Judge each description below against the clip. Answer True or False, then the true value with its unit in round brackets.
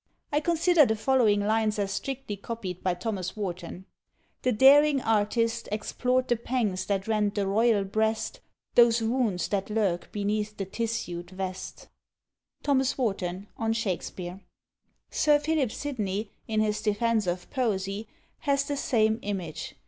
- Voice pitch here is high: True (215 Hz)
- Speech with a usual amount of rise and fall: True (3.4 semitones)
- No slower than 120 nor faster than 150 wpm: True (140 wpm)